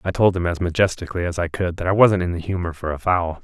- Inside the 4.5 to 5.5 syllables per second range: No, 6.6 syllables/s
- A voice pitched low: Yes, very low, 90 Hz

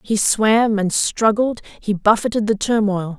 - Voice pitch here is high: Yes, high, 215 Hz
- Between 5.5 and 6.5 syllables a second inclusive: No, 4.1 syllables/s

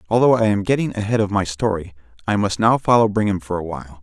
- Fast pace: Yes, fast, 240 wpm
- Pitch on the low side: Yes, low, 105 Hz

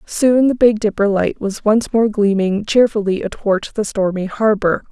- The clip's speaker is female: Yes, female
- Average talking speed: Yes, average, 170 wpm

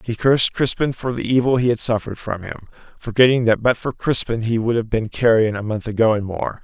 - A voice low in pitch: Yes, low, 115 Hz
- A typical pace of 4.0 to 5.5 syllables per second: No, 5.9 syllables/s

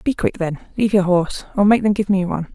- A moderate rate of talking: No, fast, 285 wpm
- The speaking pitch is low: No, high, 195 Hz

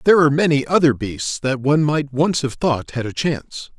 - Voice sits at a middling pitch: Yes, medium, 145 Hz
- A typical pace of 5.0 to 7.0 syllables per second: Yes, 5.5 syllables/s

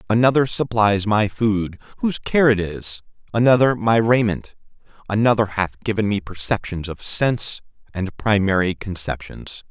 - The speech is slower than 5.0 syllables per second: Yes, 4.7 syllables/s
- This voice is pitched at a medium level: No, low, 110 Hz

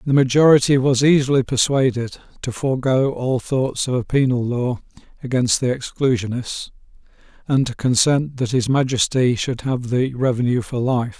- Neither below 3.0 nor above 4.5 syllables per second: No, 4.9 syllables/s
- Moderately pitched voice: No, low, 130 Hz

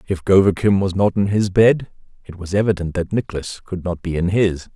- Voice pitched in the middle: No, very low, 95 Hz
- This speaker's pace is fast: Yes, fast, 215 wpm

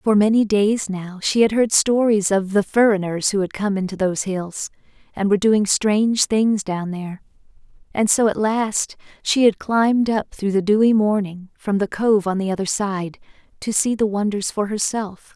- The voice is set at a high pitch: Yes, high, 205 Hz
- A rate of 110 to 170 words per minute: No, average, 190 wpm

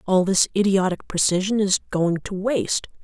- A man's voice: No, female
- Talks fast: No, average, 160 wpm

